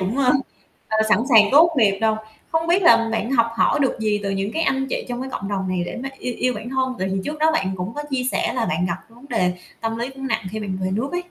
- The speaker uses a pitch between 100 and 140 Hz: No, high, 230 Hz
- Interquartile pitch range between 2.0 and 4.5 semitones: No, average, 5.3 semitones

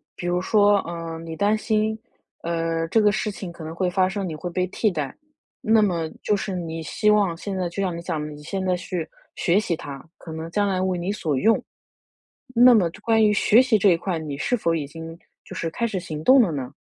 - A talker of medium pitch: Yes, medium, 180 Hz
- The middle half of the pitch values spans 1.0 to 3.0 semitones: No, average, 4.0 semitones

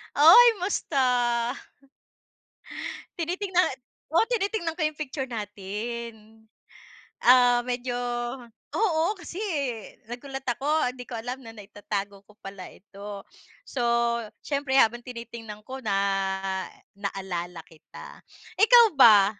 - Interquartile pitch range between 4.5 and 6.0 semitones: Yes, wide, 5.5 semitones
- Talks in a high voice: Yes, high, 245 Hz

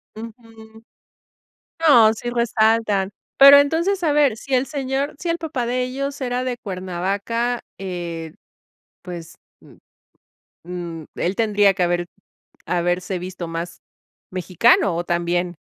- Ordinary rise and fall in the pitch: No, wide, 6.1 semitones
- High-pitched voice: Yes, high, 220 Hz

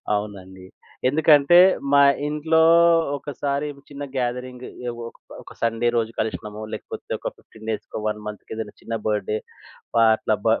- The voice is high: No, low, 115 Hz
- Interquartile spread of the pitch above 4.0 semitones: Yes, average, 4.8 semitones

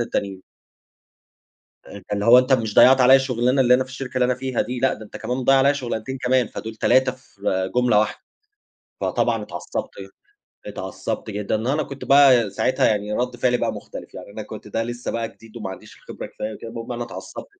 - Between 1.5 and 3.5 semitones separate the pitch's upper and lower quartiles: Yes, average, 3.2 semitones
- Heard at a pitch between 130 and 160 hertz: No, low, 120 Hz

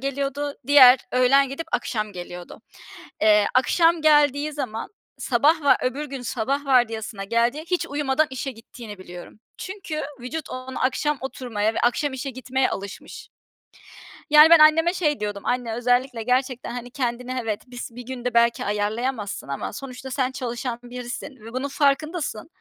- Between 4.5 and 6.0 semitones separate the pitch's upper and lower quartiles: No, average, 3.4 semitones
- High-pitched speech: Yes, very high, 255 Hz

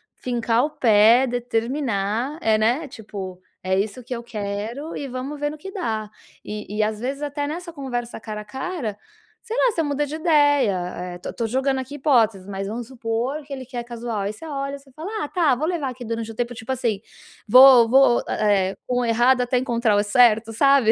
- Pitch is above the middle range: Yes, high, 245 Hz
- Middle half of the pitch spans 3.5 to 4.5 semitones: Yes, average, 4.1 semitones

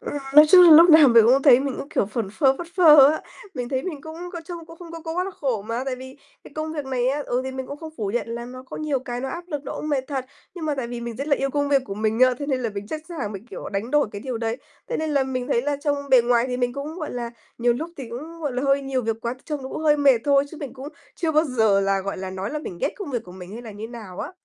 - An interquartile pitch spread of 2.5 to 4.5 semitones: Yes, average, 4.1 semitones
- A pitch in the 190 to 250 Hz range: No, very high, 265 Hz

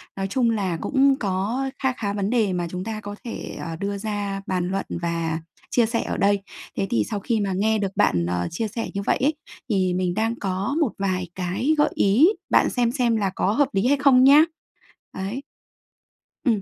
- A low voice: No, high, 205 Hz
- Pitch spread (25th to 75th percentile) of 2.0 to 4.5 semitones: Yes, average, 4.0 semitones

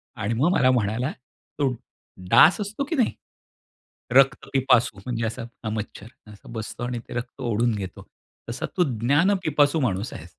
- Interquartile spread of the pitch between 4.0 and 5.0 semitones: Yes, average, 4.3 semitones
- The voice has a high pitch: No, low, 120 Hz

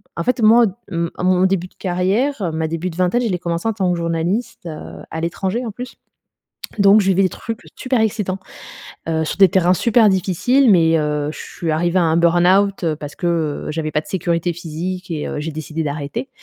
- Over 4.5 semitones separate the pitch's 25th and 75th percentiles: No, average, 3.5 semitones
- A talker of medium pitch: Yes, medium, 180 Hz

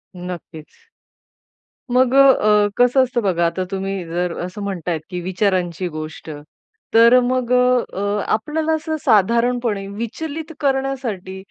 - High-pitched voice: Yes, high, 210 Hz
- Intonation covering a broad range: Yes, wide, 5.8 semitones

